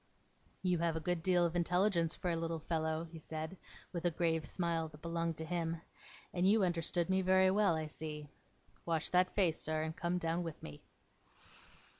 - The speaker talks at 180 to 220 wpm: Yes, average, 190 wpm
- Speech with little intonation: Yes, narrow, 1.8 semitones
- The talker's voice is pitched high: No, medium, 170 Hz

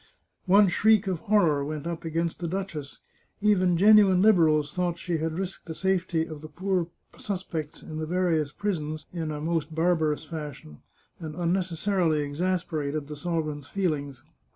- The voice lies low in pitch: No, medium, 165 Hz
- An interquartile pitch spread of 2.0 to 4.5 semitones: Yes, average, 3.3 semitones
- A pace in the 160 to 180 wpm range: No, average, 150 wpm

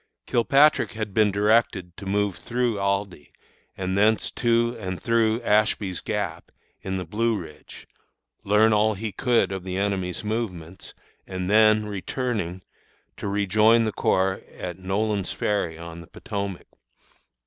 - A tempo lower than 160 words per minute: Yes, slow, 135 wpm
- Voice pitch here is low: Yes, low, 100 Hz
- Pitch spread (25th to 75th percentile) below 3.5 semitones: Yes, average, 2.8 semitones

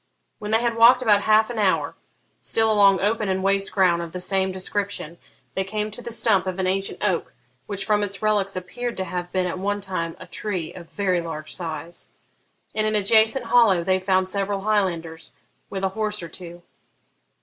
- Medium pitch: No, high, 195 Hz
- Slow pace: No, average, 195 wpm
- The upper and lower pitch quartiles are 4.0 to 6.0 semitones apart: No, average, 2.7 semitones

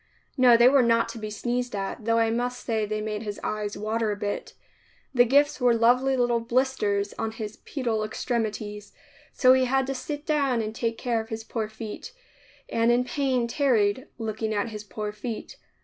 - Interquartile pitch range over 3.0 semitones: No, average, 2.7 semitones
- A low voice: No, high, 230 Hz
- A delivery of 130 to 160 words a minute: No, average, 195 wpm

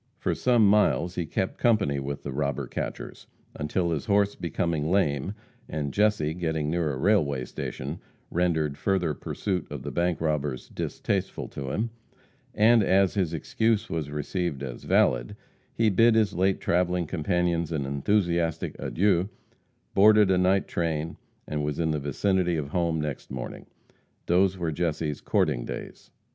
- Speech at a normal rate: Yes, average, 150 wpm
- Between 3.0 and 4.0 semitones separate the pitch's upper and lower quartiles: No, average, 4.4 semitones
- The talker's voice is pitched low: Yes, very low, 85 Hz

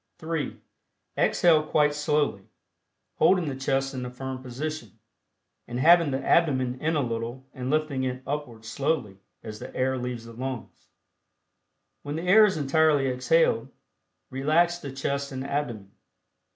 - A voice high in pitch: No, low, 135 Hz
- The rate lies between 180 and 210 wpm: No, average, 145 wpm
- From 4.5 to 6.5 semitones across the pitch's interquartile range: No, average, 3.4 semitones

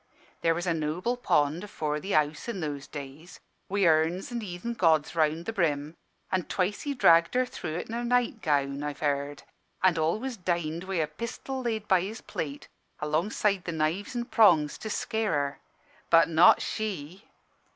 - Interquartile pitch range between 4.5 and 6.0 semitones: Yes, wide, 5.5 semitones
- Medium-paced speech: Yes, average, 180 wpm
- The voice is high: No, medium, 170 Hz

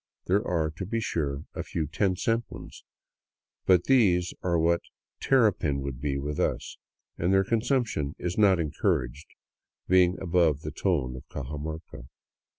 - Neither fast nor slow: Yes, average, 150 wpm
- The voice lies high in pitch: No, very low, 85 Hz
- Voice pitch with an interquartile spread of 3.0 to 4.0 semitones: No, average, 4.7 semitones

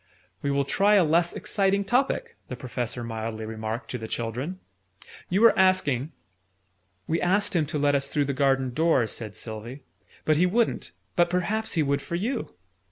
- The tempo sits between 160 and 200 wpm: Yes, average, 180 wpm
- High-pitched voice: No, medium, 145 Hz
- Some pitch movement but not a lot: No, wide, 7.7 semitones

